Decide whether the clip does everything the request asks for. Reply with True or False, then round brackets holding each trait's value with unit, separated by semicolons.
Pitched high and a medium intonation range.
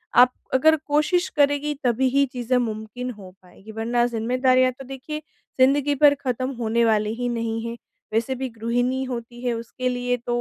False (245 Hz; 2.3 semitones)